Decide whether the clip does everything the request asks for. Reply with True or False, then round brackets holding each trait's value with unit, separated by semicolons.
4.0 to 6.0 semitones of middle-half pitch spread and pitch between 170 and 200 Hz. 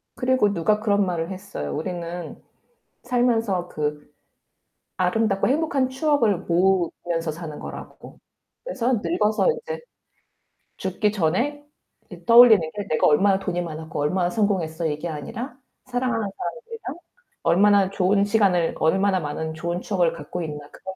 True (5.2 semitones; 190 Hz)